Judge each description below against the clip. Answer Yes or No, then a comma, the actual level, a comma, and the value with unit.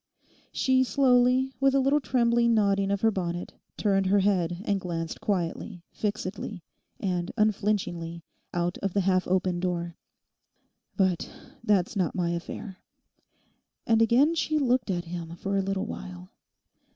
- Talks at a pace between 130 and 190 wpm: Yes, average, 140 wpm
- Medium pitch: No, high, 195 Hz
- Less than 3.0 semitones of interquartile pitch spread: No, average, 4.4 semitones